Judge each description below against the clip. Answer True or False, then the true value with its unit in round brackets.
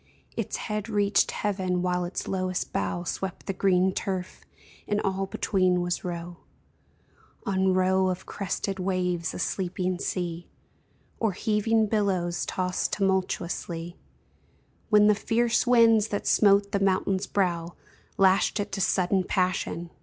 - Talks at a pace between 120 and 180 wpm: True (140 wpm)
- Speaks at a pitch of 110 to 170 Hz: False (190 Hz)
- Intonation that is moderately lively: False (2.0 semitones)